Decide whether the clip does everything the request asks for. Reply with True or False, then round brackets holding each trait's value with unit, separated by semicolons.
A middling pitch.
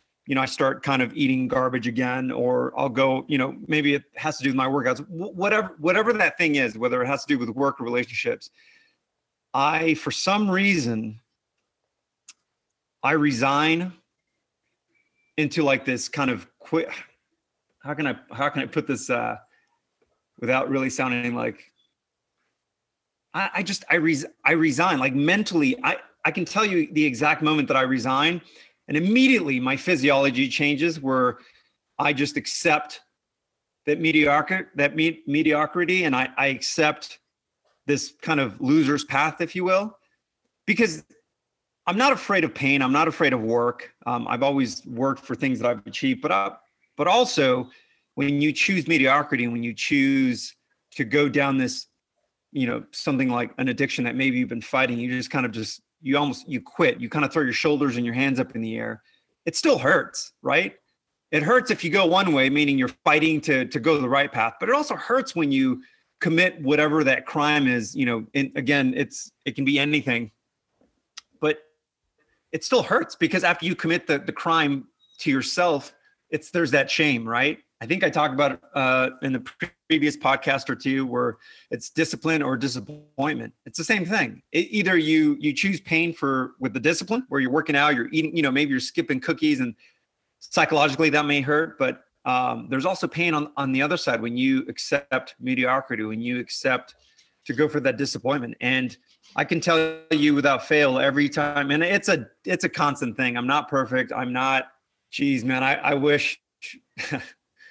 True (145 Hz)